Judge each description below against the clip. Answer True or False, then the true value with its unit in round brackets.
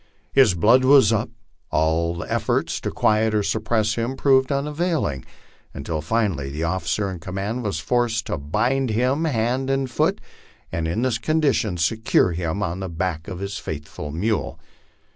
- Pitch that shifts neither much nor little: False (7.0 semitones)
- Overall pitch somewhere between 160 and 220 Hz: False (105 Hz)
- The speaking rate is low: False (165 wpm)